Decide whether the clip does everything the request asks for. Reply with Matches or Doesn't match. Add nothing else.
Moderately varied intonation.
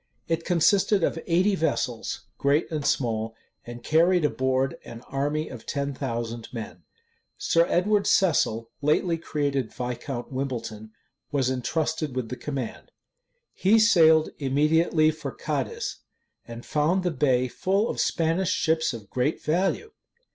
Matches